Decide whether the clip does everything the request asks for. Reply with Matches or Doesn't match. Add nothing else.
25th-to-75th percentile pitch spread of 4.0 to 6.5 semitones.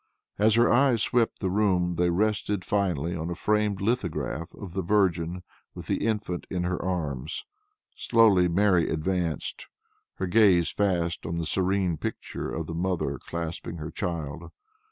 Doesn't match